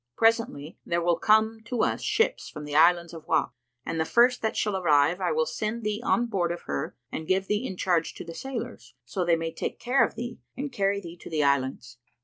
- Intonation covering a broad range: Yes, wide, 5.8 semitones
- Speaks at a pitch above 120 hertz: Yes, medium, 185 Hz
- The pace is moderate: No, fast, 230 wpm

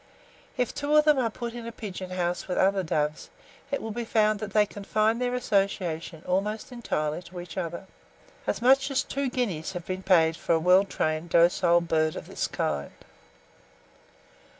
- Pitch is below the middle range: No, high, 195 Hz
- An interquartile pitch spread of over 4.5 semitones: Yes, average, 5.2 semitones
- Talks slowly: No, average, 180 wpm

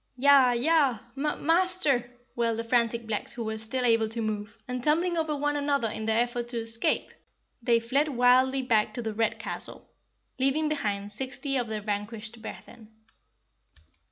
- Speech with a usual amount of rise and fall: Yes, average, 3.7 semitones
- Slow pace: No, average, 165 wpm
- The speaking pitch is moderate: No, high, 240 Hz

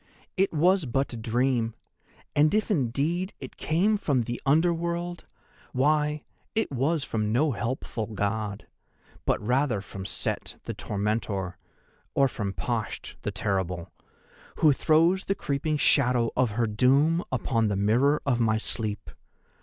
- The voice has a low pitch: Yes, low, 130 Hz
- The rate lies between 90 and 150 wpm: Yes, average, 140 wpm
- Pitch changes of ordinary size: No, wide, 5.9 semitones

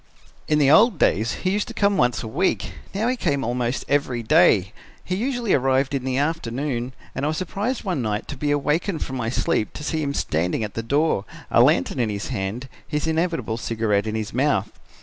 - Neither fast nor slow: No, fast, 210 wpm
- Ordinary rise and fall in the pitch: No, wide, 6.1 semitones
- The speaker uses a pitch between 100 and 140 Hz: Yes, low, 135 Hz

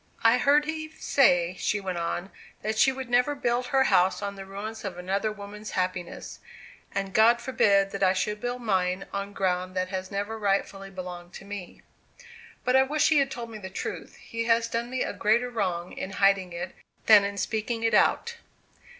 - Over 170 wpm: Yes, average, 195 wpm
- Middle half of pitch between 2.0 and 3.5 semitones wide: No, average, 4.0 semitones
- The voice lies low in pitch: No, high, 205 Hz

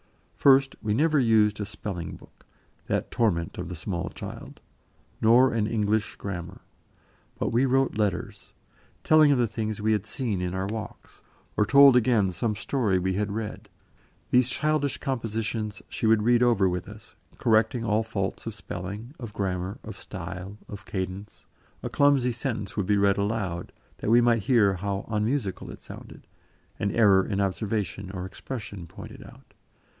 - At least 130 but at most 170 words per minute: Yes, average, 165 wpm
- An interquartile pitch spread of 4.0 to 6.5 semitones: No, average, 3.3 semitones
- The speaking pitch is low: Yes, low, 105 Hz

